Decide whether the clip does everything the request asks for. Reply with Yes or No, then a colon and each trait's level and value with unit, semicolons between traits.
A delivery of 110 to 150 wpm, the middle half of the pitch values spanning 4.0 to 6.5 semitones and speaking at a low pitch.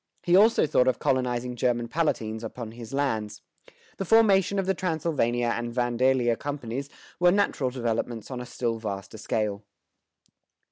Yes: average, 145 wpm; average, 4.3 semitones; low, 125 Hz